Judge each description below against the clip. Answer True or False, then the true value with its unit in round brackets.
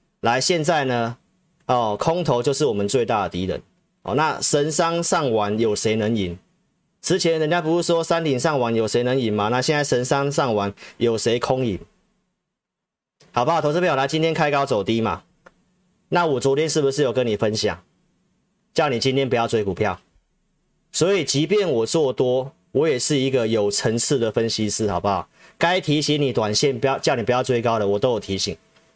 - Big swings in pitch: True (6.0 semitones)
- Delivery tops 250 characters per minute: True (270 characters per minute)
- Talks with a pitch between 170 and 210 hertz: False (135 Hz)